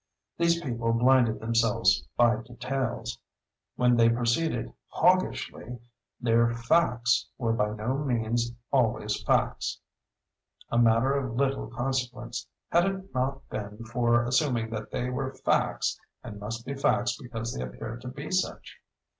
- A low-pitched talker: Yes, low, 120 Hz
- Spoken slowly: Yes, slow, 130 wpm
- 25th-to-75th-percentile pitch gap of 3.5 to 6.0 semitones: No, narrow, 2.5 semitones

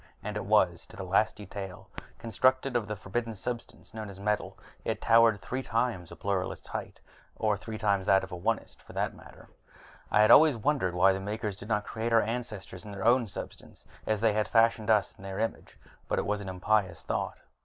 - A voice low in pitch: Yes, low, 105 Hz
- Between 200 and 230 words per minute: Yes, fast, 205 wpm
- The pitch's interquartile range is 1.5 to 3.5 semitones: Yes, average, 2.7 semitones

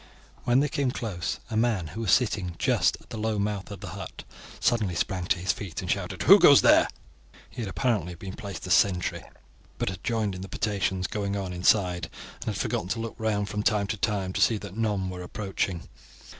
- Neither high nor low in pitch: No, low, 100 Hz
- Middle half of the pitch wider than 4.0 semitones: No, average, 3.0 semitones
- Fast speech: Yes, fast, 215 wpm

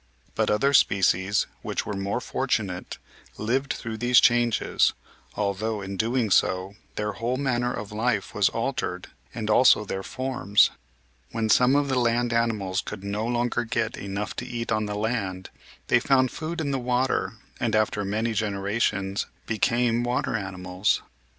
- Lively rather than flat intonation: No, average, 3.3 semitones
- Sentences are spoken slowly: No, average, 155 wpm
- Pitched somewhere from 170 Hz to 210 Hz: No, low, 110 Hz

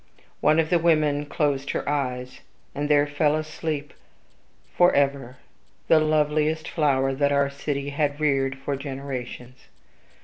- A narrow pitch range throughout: Yes, narrow, 1.9 semitones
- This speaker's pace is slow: Yes, slow, 130 wpm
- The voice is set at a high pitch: No, medium, 145 Hz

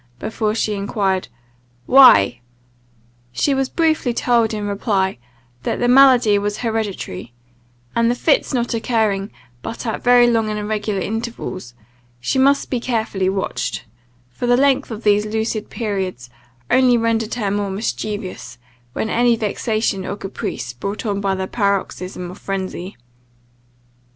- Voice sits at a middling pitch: No, high, 215 Hz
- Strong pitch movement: No, average, 3.4 semitones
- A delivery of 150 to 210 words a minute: No, slow, 135 wpm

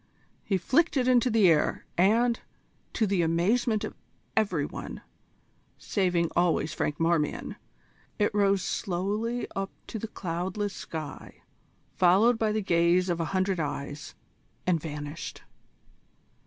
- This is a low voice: No, medium, 185 Hz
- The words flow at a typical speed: No, slow, 130 wpm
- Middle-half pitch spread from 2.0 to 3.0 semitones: No, average, 4.4 semitones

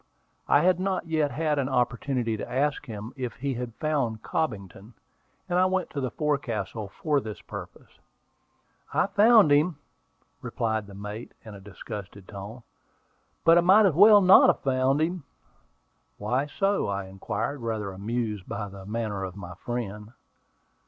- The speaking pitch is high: No, low, 125 Hz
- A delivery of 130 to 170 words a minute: Yes, average, 160 wpm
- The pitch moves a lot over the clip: Yes, wide, 6.6 semitones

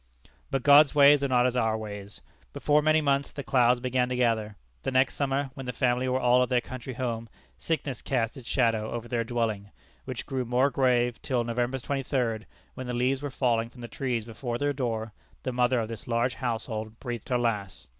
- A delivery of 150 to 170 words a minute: No, fast, 205 wpm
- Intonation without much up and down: Yes, narrow, 2.3 semitones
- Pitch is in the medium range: No, low, 125 Hz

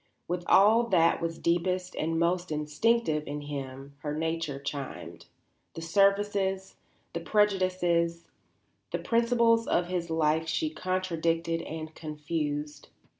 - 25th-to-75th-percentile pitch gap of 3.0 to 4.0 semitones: Yes, average, 3.4 semitones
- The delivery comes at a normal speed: No, slow, 120 wpm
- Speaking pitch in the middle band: Yes, medium, 165 Hz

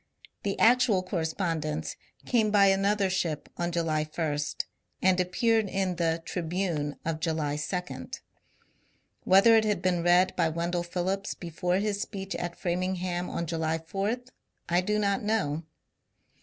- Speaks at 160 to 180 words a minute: No, average, 145 wpm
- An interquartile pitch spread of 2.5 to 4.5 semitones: Yes, average, 3.1 semitones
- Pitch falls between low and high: Yes, medium, 180 Hz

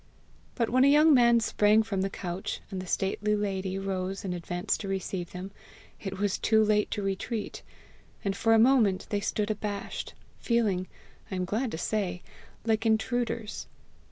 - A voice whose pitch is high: Yes, high, 205 Hz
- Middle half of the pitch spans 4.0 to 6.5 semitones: No, average, 2.7 semitones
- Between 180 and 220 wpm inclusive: No, average, 170 wpm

